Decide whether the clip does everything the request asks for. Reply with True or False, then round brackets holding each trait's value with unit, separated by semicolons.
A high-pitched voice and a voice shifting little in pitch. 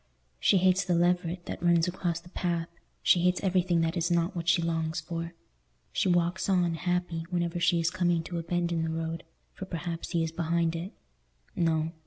False (170 Hz; 1.3 semitones)